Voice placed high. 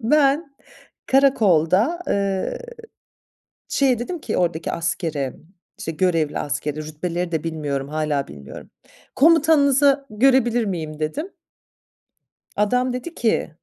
Yes: high, 195 Hz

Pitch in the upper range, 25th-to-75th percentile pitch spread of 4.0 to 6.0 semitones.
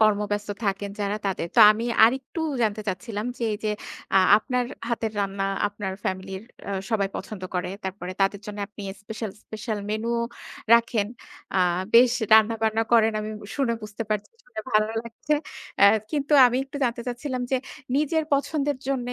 No: high, 220 Hz; average, 2.9 semitones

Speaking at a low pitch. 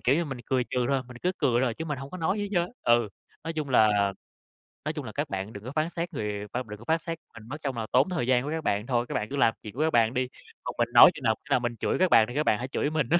Yes: low, 130 Hz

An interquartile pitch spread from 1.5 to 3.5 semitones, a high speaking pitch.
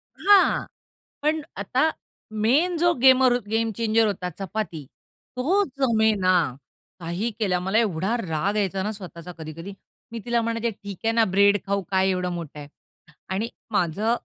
No: average, 4.2 semitones; high, 205 Hz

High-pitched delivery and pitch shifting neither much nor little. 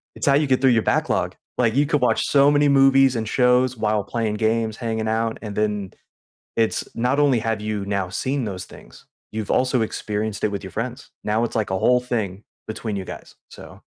No: low, 115 Hz; average, 3.2 semitones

